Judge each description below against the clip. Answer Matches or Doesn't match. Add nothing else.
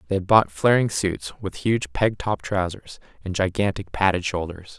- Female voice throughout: Doesn't match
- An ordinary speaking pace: Matches